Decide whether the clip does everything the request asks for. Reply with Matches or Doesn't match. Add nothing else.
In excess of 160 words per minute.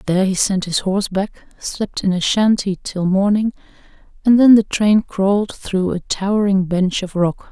Matches